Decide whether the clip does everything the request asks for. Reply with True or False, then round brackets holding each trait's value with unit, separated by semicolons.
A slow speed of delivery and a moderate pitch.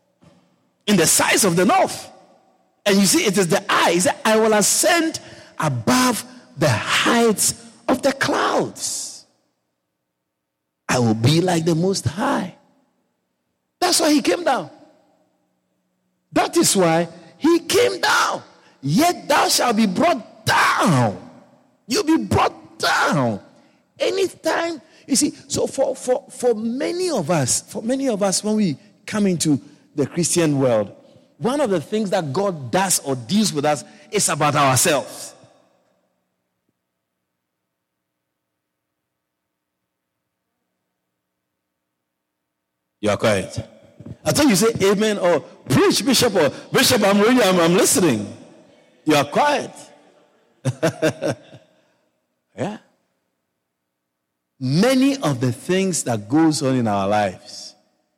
True (120 wpm; 160 Hz)